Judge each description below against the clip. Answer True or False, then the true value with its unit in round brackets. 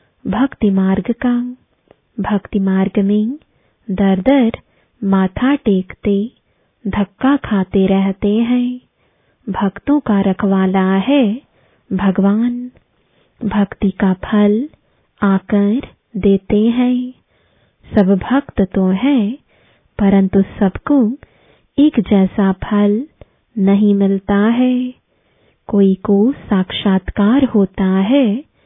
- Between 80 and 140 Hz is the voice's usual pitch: False (205 Hz)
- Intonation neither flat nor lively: True (4.0 semitones)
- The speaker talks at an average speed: False (90 wpm)